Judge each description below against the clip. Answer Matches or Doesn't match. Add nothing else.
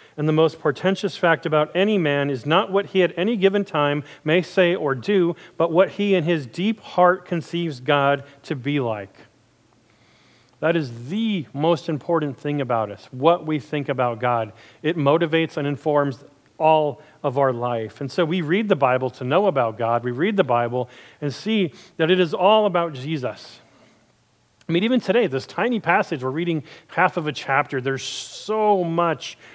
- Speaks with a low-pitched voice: Doesn't match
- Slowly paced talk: Doesn't match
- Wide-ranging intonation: Doesn't match